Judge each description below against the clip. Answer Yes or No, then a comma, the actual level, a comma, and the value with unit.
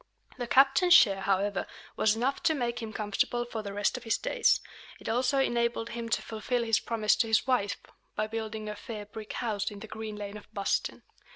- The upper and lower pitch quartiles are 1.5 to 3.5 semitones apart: Yes, narrow, 2.4 semitones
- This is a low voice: No, high, 220 Hz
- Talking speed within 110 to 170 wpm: No, fast, 205 wpm